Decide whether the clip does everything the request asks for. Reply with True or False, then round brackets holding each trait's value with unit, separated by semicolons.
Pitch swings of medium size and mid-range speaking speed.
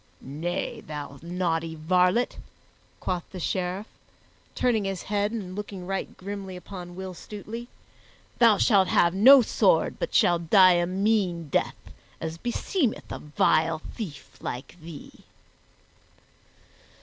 False (3.5 semitones; 125 wpm)